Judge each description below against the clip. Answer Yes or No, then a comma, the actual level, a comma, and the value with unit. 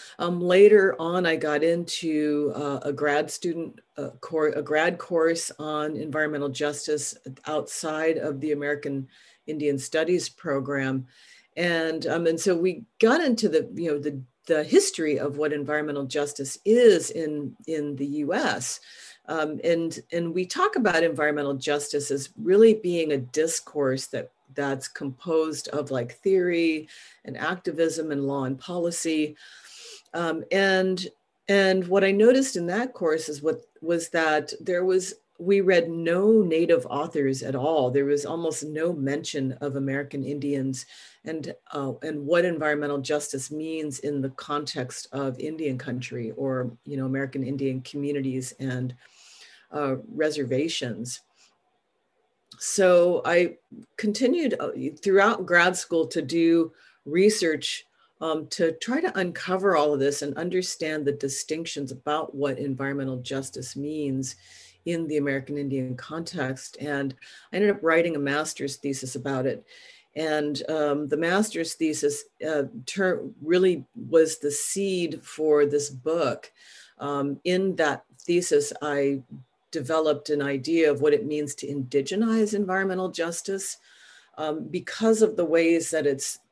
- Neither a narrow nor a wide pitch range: Yes, average, 3.3 semitones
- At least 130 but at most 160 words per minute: Yes, average, 140 wpm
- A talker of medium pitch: Yes, medium, 155 Hz